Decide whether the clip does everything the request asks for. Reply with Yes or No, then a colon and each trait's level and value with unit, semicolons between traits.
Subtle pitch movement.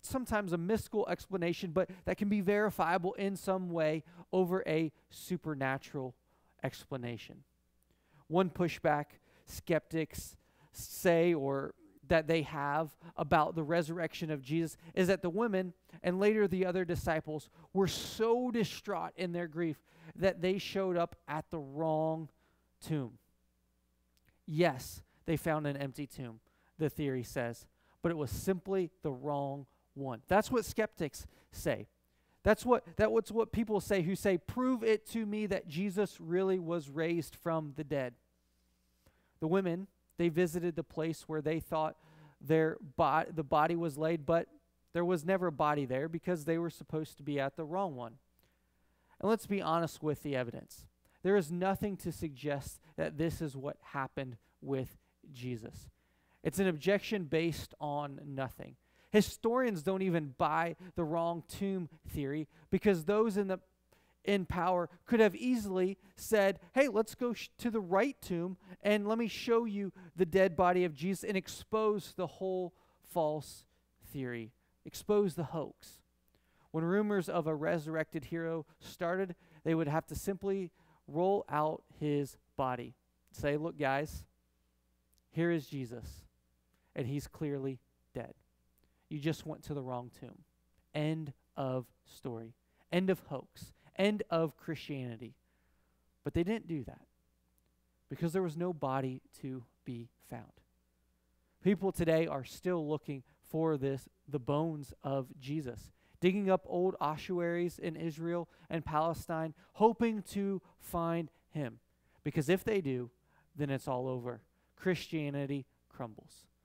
No: average, 5.3 semitones